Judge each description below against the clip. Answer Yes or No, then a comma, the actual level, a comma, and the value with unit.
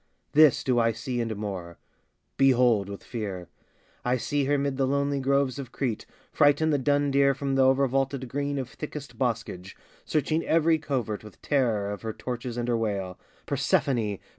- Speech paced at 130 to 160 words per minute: No, average, 170 wpm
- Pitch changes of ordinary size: Yes, average, 3.8 semitones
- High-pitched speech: No, low, 130 Hz